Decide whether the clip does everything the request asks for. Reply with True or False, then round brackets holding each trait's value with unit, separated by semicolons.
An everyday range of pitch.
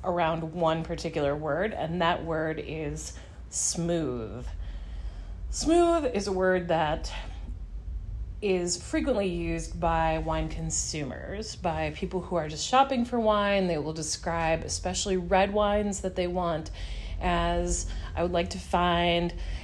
True (4.0 semitones)